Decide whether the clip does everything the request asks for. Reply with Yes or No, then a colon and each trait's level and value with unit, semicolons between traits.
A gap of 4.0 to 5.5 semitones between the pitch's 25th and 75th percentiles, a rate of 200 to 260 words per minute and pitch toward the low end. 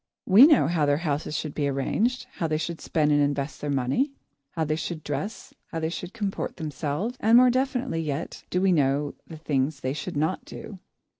No: average, 5.1 semitones; fast, 205 wpm; medium, 160 Hz